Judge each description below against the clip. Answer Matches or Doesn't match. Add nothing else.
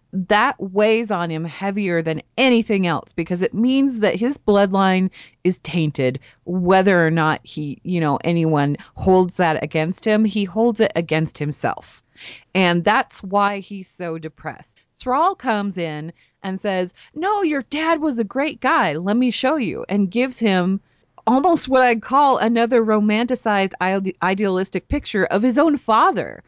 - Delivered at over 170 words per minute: Doesn't match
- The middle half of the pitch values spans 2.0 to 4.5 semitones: Doesn't match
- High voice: Matches